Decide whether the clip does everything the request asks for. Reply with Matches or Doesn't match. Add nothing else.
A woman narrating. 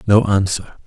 Doesn't match